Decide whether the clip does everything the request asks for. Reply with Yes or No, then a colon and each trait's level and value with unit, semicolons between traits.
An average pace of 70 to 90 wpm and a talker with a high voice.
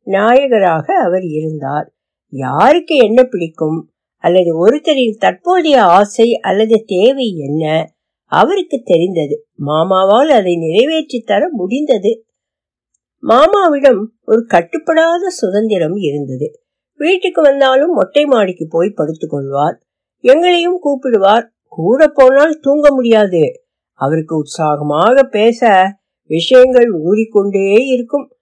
Yes: average, 85 wpm; high, 230 Hz